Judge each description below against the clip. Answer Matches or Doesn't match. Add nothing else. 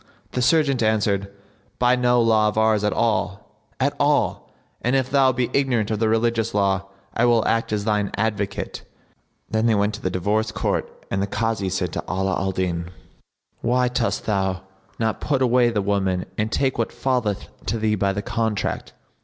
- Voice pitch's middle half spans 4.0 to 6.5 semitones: Doesn't match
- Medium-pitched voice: Doesn't match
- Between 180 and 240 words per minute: Matches